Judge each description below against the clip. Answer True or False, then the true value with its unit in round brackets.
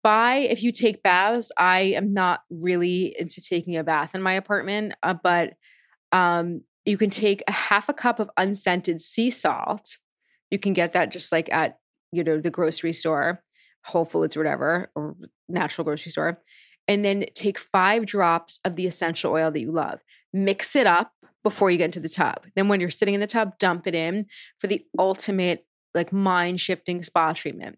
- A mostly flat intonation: False (3.1 semitones)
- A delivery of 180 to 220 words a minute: True (190 wpm)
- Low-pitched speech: False (180 Hz)